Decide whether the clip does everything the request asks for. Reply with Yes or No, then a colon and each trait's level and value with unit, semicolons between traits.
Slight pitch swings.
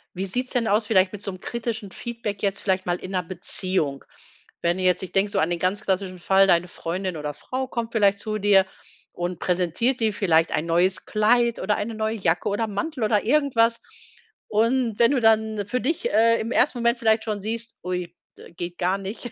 No: average, 3.8 semitones